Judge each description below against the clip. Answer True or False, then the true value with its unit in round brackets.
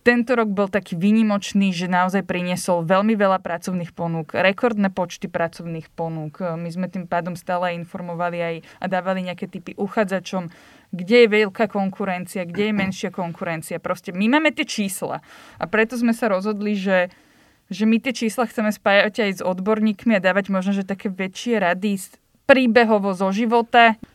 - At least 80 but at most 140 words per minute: False (160 wpm)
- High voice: True (195 Hz)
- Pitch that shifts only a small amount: False (3.2 semitones)